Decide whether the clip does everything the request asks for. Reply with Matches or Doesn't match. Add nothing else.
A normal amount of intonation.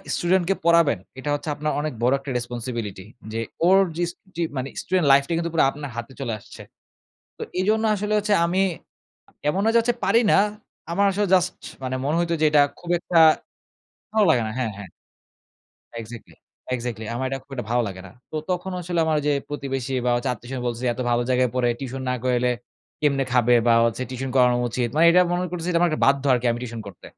Doesn't match